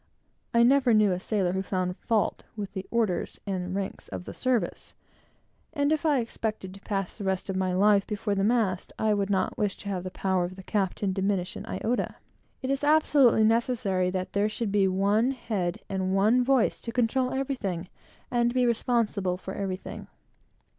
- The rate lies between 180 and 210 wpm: Yes, average, 190 wpm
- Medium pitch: No, high, 205 Hz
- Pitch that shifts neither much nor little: Yes, average, 3.8 semitones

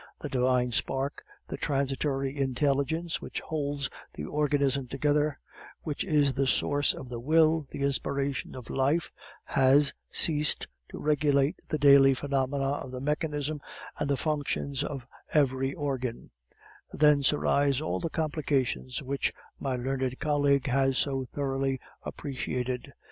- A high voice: No, medium, 140 Hz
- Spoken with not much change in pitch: Yes, narrow, 1.8 semitones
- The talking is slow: Yes, slow, 130 wpm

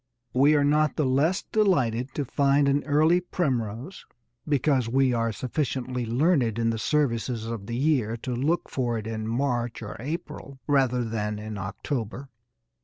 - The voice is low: Yes, low, 130 Hz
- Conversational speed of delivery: Yes, average, 160 wpm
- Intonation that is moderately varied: Yes, average, 4.0 semitones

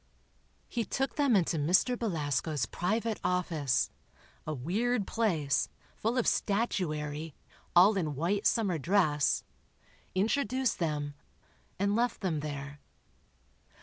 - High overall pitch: No, medium, 180 Hz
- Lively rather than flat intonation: Yes, wide, 6.7 semitones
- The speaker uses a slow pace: Yes, slow, 100 wpm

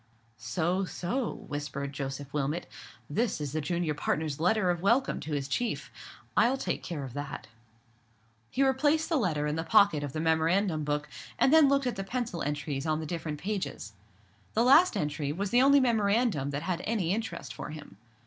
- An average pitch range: No, wide, 7.3 semitones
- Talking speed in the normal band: Yes, average, 185 wpm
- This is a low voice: No, medium, 165 Hz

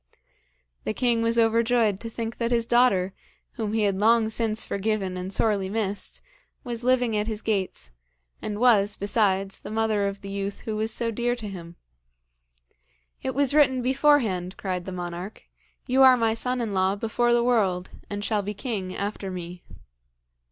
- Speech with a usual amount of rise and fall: Yes, average, 3.2 semitones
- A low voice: No, high, 215 Hz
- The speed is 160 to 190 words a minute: Yes, average, 175 wpm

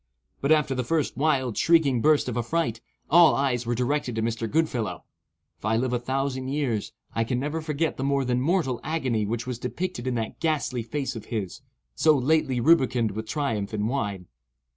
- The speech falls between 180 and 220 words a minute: Yes, average, 190 wpm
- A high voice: No, low, 130 Hz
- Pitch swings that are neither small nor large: Yes, average, 4.4 semitones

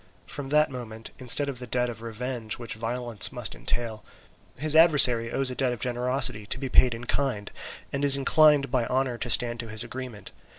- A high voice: No, low, 125 Hz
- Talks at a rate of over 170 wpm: Yes, average, 200 wpm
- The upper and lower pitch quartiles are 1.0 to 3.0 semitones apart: Yes, average, 2.7 semitones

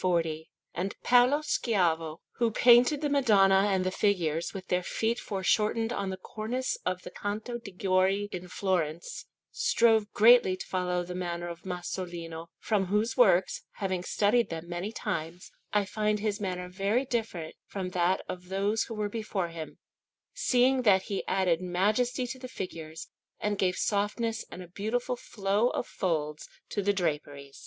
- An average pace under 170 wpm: Yes, average, 160 wpm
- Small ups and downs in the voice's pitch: No, average, 3.8 semitones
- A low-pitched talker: No, high, 195 Hz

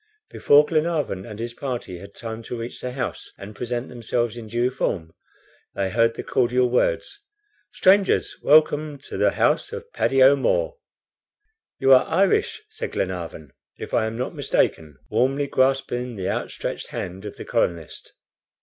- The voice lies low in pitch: Yes, low, 125 Hz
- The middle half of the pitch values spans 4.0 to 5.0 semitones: Yes, average, 4.7 semitones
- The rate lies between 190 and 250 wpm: No, average, 155 wpm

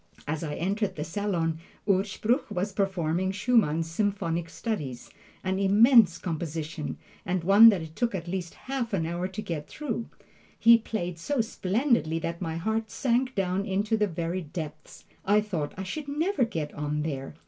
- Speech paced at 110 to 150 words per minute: No, average, 165 wpm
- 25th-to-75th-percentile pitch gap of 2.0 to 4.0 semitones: No, average, 5.0 semitones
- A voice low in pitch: No, high, 190 Hz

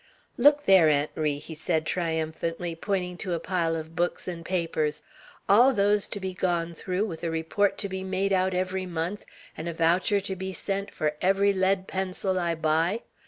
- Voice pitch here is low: No, medium, 180 Hz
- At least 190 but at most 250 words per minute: Yes, average, 195 wpm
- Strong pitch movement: No, average, 2.8 semitones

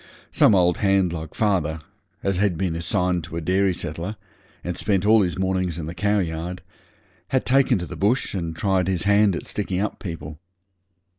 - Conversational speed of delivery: Yes, average, 180 wpm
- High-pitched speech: No, very low, 90 Hz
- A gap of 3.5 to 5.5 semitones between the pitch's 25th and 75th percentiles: No, average, 3.0 semitones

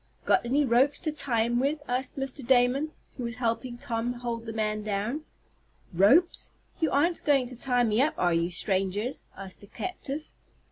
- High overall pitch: Yes, high, 245 Hz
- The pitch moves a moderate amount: Yes, average, 3.9 semitones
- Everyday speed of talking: Yes, average, 180 wpm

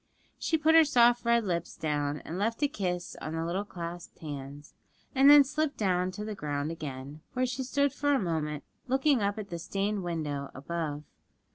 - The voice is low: No, medium, 185 Hz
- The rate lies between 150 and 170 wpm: No, average, 190 wpm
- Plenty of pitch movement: Yes, wide, 8.5 semitones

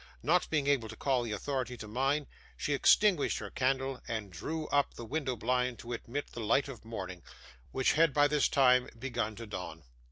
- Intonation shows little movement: No, average, 3.9 semitones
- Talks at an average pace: Yes, average, 195 wpm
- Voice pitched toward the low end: Yes, low, 130 Hz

